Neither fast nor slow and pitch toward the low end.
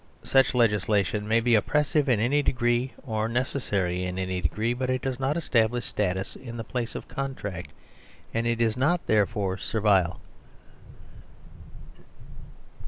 Yes: average, 145 wpm; low, 115 Hz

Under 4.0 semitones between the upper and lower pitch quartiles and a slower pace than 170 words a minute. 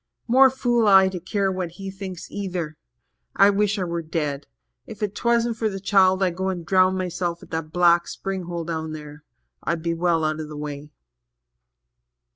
No: average, 3.0 semitones; average, 185 wpm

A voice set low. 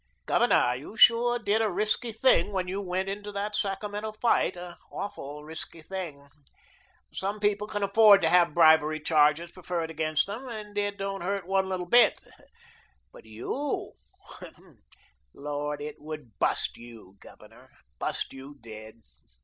No: medium, 185 Hz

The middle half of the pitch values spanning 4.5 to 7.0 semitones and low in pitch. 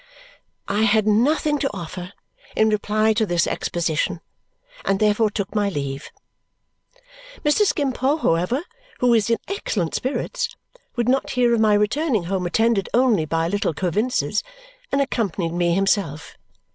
No: wide, 5.5 semitones; high, 210 Hz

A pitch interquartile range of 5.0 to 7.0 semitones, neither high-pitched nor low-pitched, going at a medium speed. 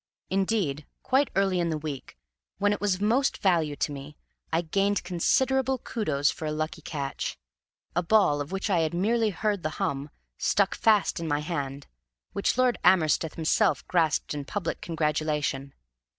Yes: average, 5.3 semitones; medium, 170 Hz; average, 165 wpm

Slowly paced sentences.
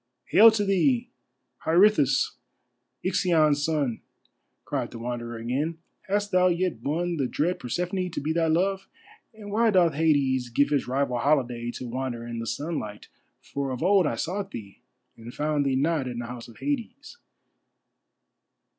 No: average, 155 wpm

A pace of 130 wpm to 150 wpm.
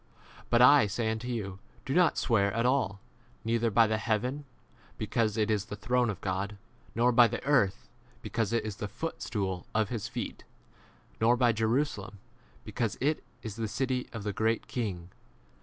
No: average, 185 wpm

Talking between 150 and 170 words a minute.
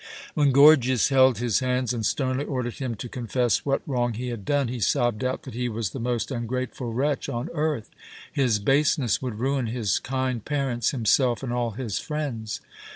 No: average, 185 wpm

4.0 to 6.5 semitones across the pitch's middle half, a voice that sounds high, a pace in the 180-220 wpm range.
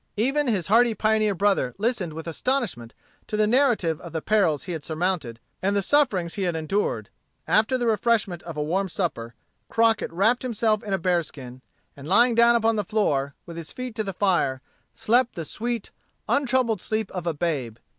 Yes: wide, 5.5 semitones; high, 200 Hz; average, 185 wpm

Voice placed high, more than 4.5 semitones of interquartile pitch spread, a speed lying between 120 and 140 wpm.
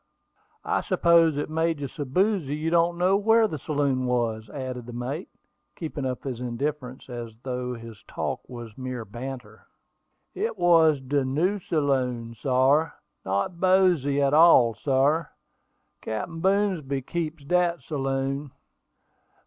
No: medium, 140 Hz; average, 4.9 semitones; slow, 135 wpm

